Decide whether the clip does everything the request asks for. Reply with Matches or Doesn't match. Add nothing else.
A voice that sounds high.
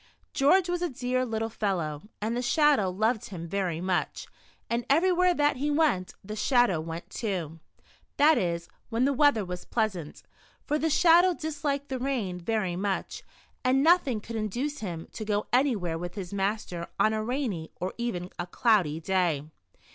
Matches